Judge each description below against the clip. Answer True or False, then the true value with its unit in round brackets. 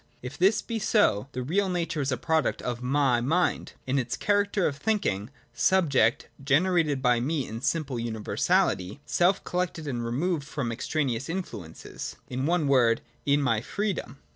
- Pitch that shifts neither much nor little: False (6.3 semitones)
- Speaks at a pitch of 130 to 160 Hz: True (140 Hz)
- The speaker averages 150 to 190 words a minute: True (165 wpm)